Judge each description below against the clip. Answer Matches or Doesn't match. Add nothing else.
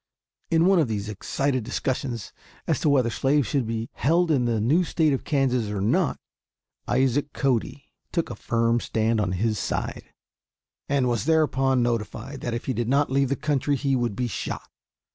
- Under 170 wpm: Doesn't match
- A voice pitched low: Matches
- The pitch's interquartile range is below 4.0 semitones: Matches